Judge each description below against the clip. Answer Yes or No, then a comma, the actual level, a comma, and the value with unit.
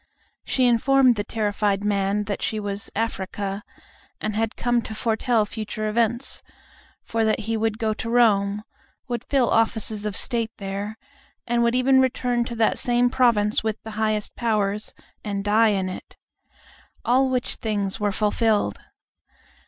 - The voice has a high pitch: Yes, high, 220 Hz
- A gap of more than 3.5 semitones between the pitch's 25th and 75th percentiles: No, narrow, 2.4 semitones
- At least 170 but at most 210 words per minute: No, average, 150 wpm